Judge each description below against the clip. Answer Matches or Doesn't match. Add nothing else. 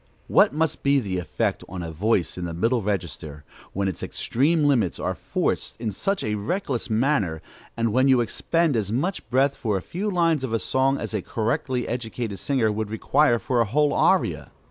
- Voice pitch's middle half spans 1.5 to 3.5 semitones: Doesn't match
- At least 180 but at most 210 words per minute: Matches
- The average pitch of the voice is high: Doesn't match